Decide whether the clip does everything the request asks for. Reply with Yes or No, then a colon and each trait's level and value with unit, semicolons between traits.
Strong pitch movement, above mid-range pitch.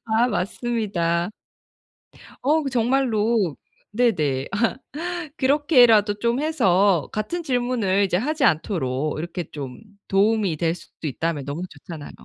Yes: wide, 6.4 semitones; high, 205 Hz